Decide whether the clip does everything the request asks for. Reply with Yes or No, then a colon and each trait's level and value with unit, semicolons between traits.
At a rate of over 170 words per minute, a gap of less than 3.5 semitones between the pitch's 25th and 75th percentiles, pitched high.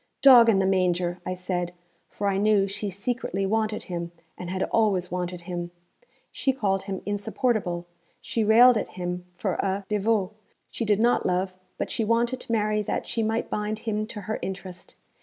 Yes: average, 180 wpm; average, 3.1 semitones; high, 200 Hz